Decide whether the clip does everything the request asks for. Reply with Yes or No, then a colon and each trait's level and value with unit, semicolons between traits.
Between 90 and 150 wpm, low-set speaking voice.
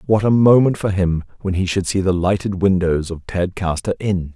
No: fast, 205 wpm; very low, 95 Hz